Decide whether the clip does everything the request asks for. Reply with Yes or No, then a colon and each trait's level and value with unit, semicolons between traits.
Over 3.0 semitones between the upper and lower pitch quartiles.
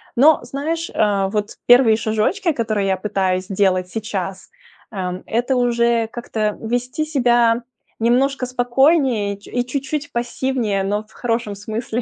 Yes: average, 3.5 semitones